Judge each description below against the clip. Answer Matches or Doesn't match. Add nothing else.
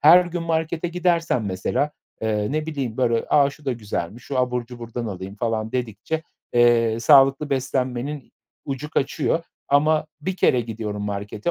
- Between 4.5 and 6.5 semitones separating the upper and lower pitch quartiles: Matches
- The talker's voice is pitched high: Doesn't match